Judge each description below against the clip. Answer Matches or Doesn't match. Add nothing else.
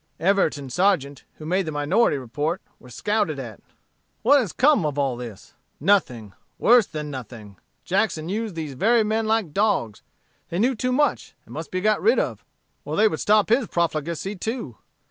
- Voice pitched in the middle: Matches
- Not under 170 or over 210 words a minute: Matches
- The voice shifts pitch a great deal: Matches